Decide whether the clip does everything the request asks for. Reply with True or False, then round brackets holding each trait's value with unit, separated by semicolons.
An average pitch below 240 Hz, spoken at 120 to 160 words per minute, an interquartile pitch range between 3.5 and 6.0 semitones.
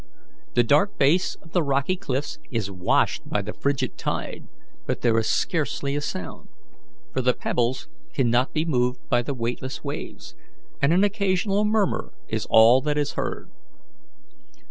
True (140 Hz; 155 wpm; 5.3 semitones)